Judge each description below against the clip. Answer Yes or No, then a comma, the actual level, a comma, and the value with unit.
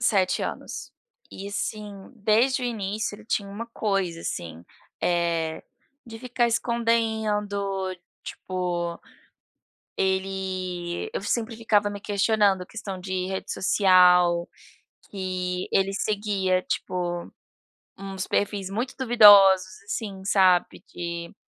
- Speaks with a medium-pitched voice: No, high, 195 Hz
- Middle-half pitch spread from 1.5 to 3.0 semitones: Yes, narrow, 2.6 semitones